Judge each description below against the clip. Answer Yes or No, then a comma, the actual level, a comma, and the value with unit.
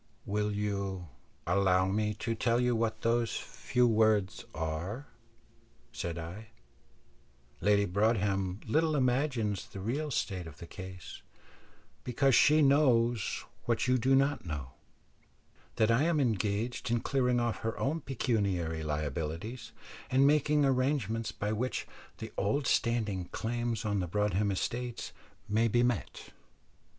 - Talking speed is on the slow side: Yes, slow, 130 wpm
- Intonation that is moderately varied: Yes, average, 4.2 semitones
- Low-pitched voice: Yes, low, 110 Hz